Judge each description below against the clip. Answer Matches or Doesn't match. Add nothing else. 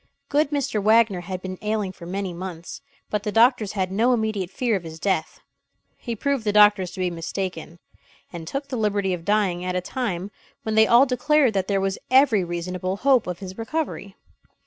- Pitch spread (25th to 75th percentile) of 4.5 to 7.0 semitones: Doesn't match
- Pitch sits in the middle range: Doesn't match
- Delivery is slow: Doesn't match